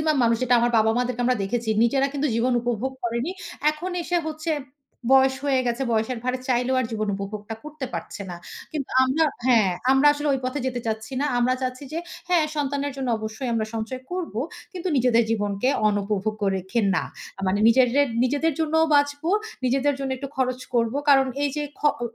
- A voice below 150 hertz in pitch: No, very high, 255 Hz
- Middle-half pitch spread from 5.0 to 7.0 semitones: No, average, 3.9 semitones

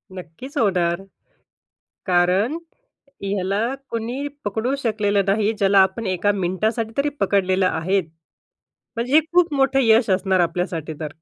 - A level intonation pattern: No, average, 3.7 semitones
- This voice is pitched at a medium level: No, high, 200 Hz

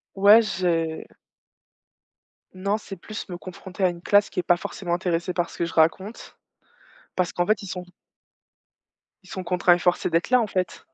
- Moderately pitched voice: Yes, medium, 180 Hz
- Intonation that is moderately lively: No, narrow, 2.3 semitones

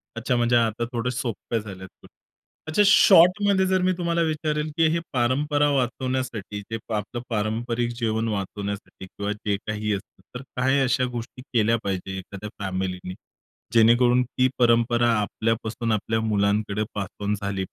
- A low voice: Yes, low, 115 Hz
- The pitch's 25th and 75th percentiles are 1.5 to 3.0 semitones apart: No, average, 3.7 semitones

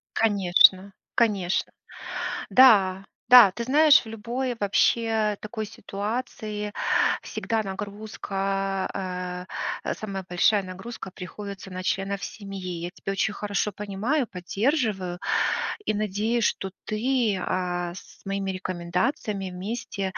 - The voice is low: No, high, 200 Hz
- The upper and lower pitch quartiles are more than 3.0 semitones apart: No, average, 2.7 semitones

